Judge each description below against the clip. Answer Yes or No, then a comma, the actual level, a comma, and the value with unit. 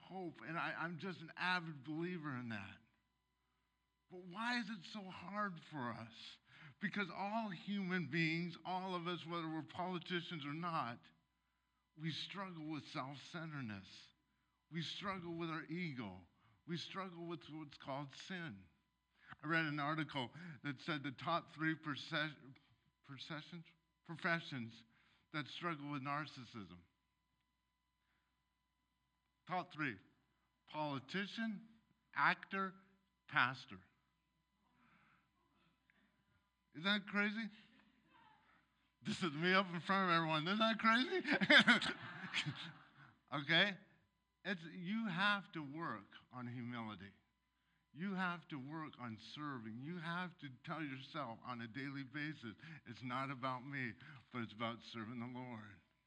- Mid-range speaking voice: Yes, medium, 155 Hz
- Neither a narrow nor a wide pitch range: No, wide, 6.2 semitones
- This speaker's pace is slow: Yes, slow, 120 wpm